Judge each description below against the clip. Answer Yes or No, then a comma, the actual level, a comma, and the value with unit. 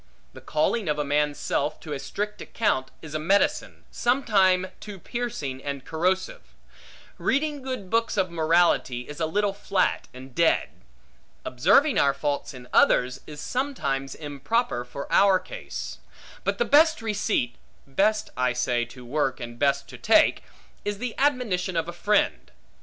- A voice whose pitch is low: No, medium, 170 Hz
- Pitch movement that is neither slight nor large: No, wide, 7.2 semitones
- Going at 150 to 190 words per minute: Yes, average, 155 wpm